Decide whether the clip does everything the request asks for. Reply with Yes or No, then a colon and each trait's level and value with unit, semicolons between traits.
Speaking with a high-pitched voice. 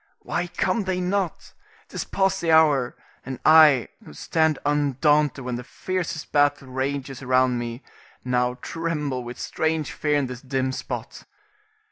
No: medium, 145 Hz